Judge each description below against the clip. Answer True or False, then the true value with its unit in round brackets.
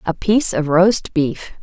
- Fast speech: False (185 wpm)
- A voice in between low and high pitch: True (180 Hz)